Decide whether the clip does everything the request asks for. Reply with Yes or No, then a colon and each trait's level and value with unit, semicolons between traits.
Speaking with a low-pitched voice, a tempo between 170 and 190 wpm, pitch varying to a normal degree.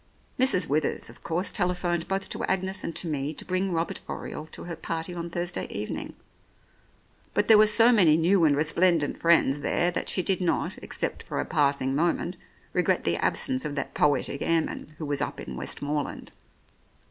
No: medium, 170 Hz; average, 180 wpm; average, 3.6 semitones